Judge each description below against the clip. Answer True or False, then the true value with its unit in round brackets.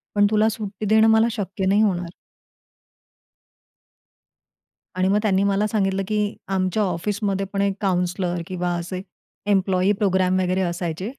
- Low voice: False (195 Hz)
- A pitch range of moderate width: False (2.1 semitones)